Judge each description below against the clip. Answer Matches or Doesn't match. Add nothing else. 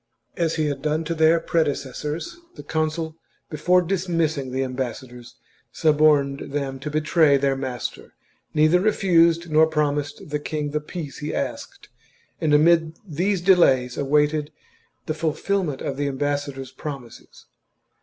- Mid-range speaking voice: Matches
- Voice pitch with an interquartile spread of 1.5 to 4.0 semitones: Matches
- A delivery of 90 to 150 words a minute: Matches